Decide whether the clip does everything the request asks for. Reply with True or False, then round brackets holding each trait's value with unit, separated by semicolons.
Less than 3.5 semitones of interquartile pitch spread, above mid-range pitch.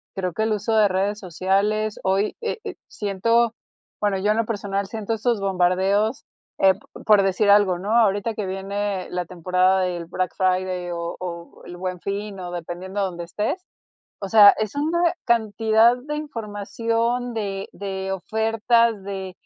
True (2.9 semitones; 200 Hz)